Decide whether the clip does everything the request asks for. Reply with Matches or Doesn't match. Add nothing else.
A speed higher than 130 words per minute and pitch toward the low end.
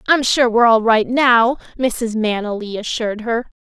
Doesn't match